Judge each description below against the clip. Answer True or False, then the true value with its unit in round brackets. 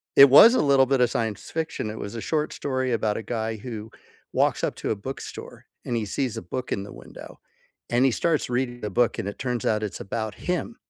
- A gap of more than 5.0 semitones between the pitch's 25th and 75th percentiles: False (3.6 semitones)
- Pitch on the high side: False (120 Hz)